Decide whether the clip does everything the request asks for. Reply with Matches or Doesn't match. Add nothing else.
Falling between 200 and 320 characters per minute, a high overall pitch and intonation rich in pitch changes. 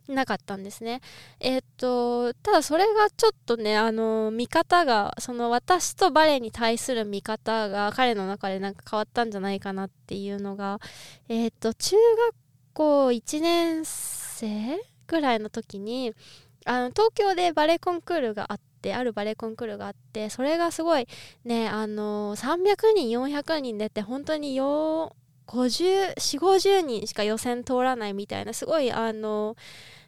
Matches